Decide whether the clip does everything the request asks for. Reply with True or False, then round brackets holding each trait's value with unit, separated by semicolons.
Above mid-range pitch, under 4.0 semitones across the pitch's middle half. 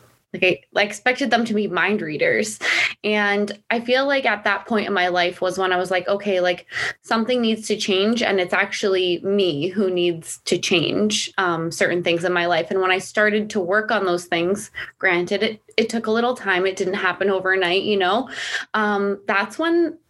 True (200 Hz; 2.8 semitones)